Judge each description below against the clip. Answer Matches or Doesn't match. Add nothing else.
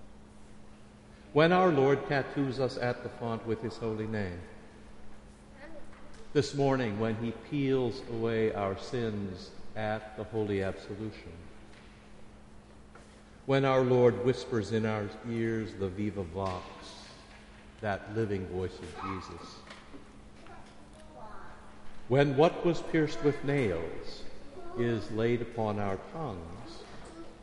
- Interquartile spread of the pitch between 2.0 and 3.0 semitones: Doesn't match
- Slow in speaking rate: Matches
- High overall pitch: Doesn't match